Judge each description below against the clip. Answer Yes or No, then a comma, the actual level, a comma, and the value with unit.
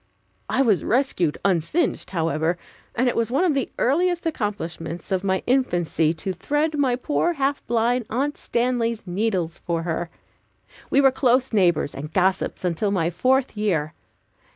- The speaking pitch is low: No, high, 215 Hz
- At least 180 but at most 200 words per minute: No, average, 155 wpm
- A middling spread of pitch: No, wide, 7.3 semitones